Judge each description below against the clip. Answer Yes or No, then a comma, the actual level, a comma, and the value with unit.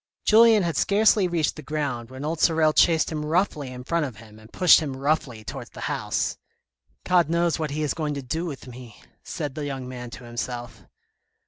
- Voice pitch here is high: No, medium, 150 Hz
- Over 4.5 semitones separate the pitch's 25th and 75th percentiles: Yes, average, 4.9 semitones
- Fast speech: Yes, fast, 210 wpm